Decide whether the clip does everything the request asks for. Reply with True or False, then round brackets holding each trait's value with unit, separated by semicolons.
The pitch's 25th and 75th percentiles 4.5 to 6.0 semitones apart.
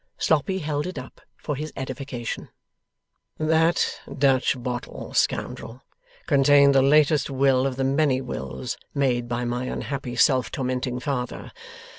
False (2.4 semitones)